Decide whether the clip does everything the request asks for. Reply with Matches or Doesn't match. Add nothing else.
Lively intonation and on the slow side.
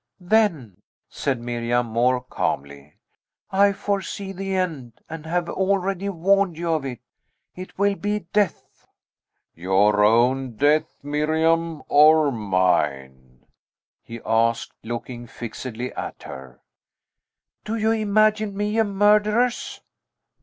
Matches